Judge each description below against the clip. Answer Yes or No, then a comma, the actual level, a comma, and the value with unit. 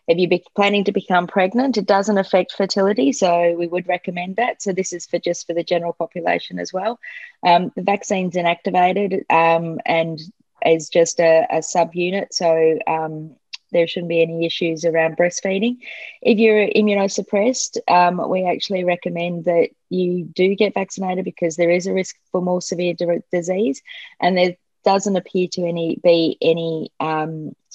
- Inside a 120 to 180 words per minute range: Yes, average, 165 wpm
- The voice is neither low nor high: Yes, medium, 180 Hz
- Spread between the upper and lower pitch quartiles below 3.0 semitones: Yes, narrow, 2.6 semitones